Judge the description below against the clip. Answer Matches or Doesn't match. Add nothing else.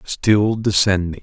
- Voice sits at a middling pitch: Doesn't match